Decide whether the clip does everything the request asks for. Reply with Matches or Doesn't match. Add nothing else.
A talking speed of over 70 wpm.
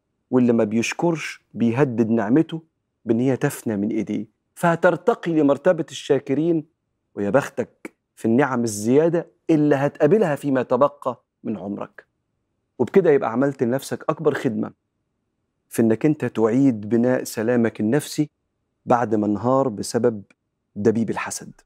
Matches